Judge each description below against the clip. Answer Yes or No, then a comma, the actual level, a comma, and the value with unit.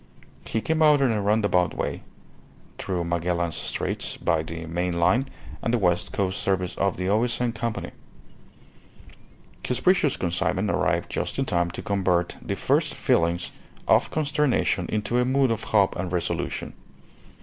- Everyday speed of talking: Yes, average, 150 wpm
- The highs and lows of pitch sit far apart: Yes, wide, 5.7 semitones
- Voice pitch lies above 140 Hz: No, low, 100 Hz